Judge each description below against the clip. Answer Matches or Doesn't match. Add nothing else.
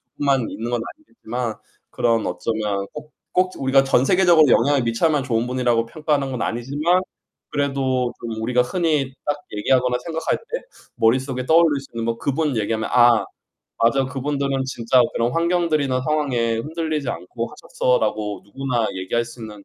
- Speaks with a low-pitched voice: Matches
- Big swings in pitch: Doesn't match